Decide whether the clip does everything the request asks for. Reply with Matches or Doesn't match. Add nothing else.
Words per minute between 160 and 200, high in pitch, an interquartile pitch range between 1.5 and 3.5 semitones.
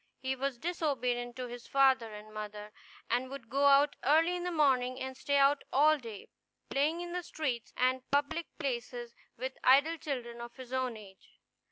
Matches